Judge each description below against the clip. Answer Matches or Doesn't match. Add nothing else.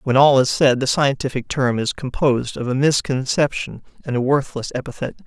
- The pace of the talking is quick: Doesn't match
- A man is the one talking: Matches